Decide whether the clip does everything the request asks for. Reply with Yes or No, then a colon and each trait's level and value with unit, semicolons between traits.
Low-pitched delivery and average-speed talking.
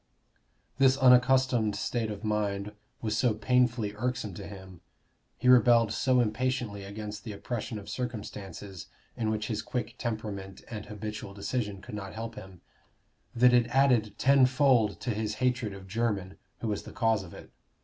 Yes: low, 110 Hz; average, 160 wpm